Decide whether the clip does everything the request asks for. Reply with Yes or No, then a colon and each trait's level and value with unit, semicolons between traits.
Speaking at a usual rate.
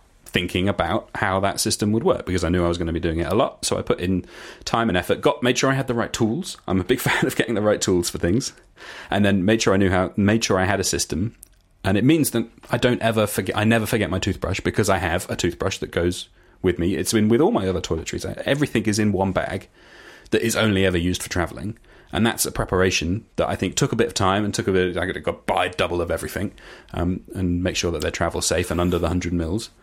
No: fast, 280 wpm